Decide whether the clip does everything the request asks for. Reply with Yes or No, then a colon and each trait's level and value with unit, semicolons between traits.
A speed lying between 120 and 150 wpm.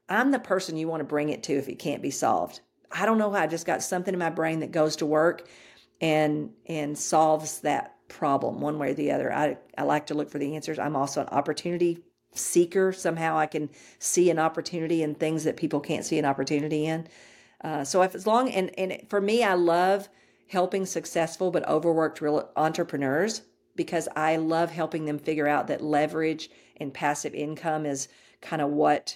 No: fast, 205 wpm